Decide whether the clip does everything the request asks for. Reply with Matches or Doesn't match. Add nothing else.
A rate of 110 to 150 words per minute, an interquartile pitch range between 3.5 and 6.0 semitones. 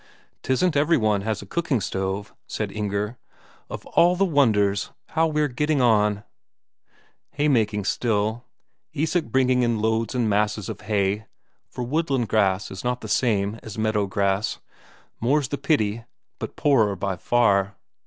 Matches